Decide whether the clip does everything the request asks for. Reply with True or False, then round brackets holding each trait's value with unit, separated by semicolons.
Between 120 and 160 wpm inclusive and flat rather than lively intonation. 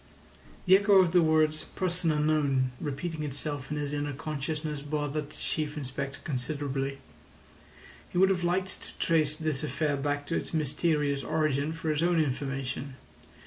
True (155 wpm; 2.2 semitones)